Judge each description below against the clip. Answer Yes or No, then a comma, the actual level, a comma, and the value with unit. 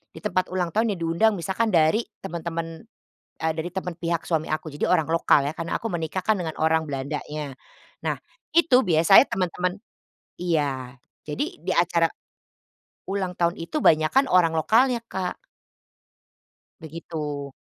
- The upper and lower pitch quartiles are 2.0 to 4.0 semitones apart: Yes, average, 3.2 semitones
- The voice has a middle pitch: Yes, medium, 170 Hz